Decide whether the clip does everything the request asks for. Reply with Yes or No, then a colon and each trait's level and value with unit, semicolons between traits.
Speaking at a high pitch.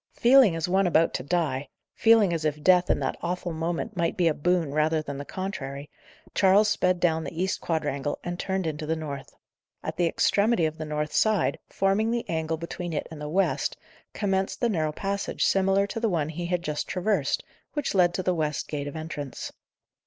No: medium, 170 Hz